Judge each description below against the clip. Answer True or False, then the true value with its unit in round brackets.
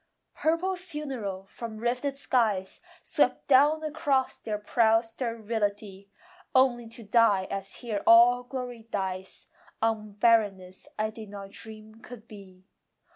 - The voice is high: True (225 Hz)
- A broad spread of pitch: False (3.4 semitones)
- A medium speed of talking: False (125 wpm)